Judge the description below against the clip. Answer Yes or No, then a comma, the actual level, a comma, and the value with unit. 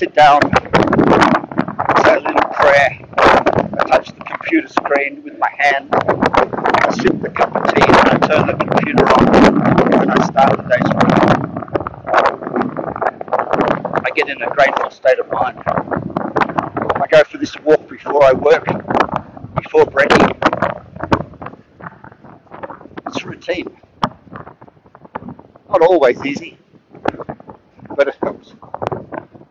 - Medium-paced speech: No, slow, 120 wpm